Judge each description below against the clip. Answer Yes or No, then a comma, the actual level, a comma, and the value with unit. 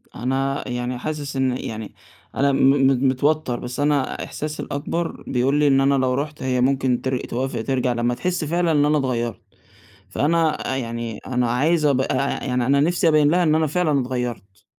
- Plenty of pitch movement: No, average, 3.2 semitones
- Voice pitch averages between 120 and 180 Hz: Yes, low, 135 Hz